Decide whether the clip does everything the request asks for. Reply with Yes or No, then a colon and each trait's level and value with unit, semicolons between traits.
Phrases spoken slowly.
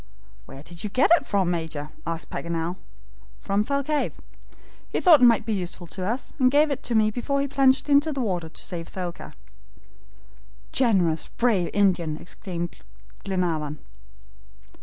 No: average, 155 wpm